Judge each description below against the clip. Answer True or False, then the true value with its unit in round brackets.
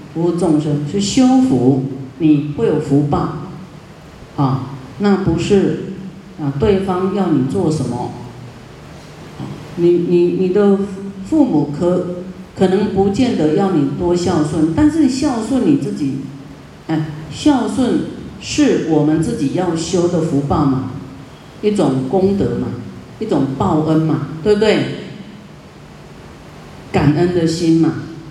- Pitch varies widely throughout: False (4.4 semitones)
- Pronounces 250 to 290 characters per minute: False (170 characters per minute)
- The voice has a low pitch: False (170 Hz)